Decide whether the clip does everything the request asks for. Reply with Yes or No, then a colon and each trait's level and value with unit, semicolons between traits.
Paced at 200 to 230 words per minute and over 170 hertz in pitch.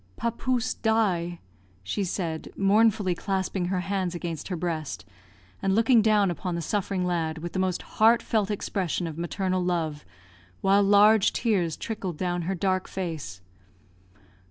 No: average, 140 wpm; medium, 185 Hz